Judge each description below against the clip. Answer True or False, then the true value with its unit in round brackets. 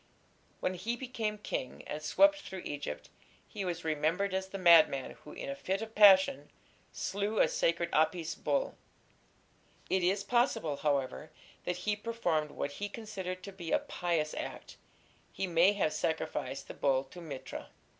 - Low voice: False (180 Hz)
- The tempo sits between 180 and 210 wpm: False (160 wpm)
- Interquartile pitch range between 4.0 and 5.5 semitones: True (4.6 semitones)